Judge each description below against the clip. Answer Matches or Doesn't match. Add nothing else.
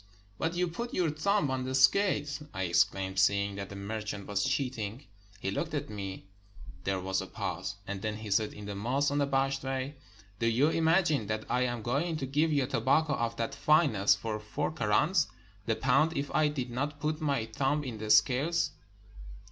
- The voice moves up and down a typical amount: Doesn't match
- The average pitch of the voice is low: Matches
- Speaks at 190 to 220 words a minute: Matches